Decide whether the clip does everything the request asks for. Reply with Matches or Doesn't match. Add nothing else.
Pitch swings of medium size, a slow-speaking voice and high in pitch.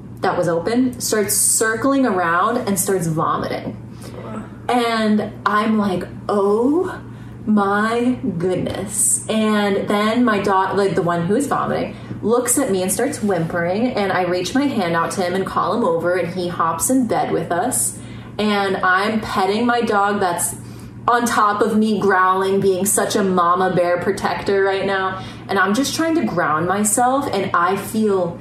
Doesn't match